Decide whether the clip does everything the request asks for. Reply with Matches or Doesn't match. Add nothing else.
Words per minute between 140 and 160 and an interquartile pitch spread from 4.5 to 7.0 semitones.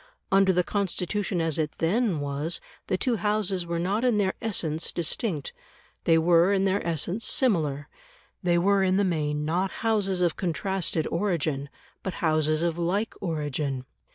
Doesn't match